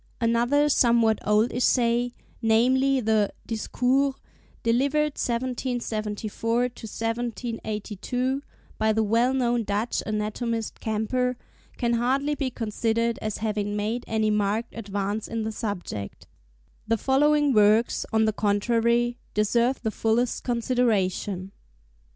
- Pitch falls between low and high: No, high, 230 Hz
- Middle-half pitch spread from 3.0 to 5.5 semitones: No, narrow, 2.4 semitones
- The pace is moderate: No, slow, 110 wpm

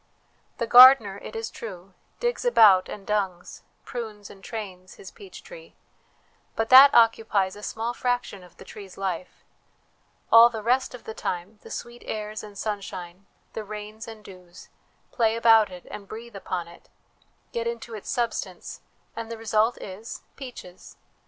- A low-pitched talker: No, high, 215 Hz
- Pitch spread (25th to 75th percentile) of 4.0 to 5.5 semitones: No, average, 3.2 semitones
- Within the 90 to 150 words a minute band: No, average, 160 wpm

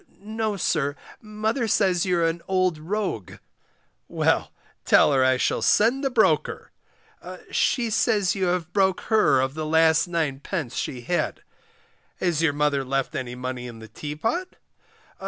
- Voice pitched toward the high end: No, medium, 170 Hz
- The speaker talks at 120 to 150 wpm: Yes, average, 145 wpm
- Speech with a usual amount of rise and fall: No, wide, 6.9 semitones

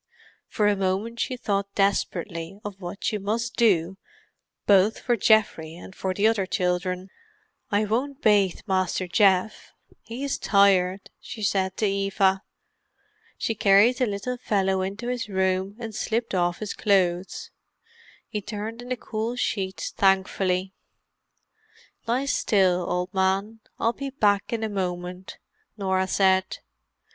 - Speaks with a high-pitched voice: Yes, high, 200 Hz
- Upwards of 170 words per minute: No, average, 140 wpm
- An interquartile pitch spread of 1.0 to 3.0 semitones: Yes, average, 2.7 semitones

